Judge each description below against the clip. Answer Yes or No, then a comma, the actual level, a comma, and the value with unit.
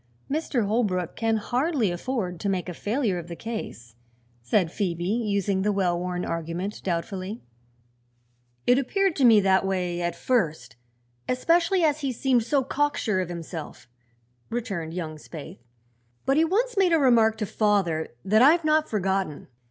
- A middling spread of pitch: No, wide, 6.4 semitones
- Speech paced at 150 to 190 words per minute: Yes, average, 155 wpm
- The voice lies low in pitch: No, high, 205 Hz